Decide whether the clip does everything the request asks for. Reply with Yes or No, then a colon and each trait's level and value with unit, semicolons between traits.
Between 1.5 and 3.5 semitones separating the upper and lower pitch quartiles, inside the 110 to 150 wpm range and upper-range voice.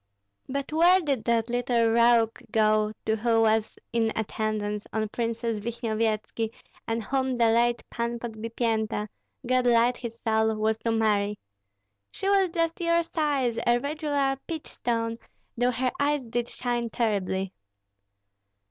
Yes: narrow, 2.4 semitones; average, 140 wpm; high, 230 Hz